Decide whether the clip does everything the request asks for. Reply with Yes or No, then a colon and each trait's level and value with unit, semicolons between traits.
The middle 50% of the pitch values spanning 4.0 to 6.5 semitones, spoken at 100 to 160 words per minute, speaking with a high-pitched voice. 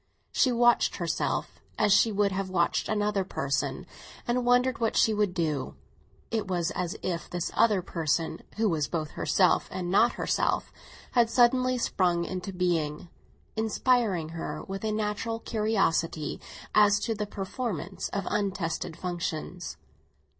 Yes: average, 4.3 semitones; average, 140 wpm; high, 195 Hz